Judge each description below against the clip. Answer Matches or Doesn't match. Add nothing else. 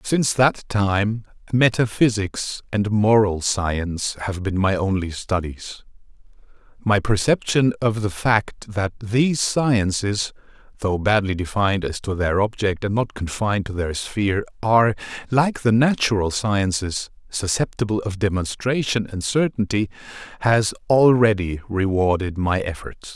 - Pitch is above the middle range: Doesn't match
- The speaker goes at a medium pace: Doesn't match